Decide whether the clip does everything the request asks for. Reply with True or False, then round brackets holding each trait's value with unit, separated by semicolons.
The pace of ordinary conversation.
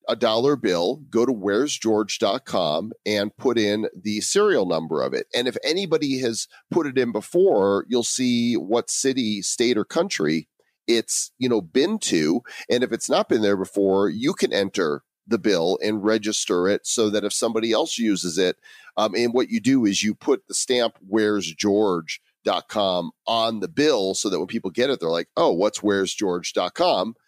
True (180 wpm)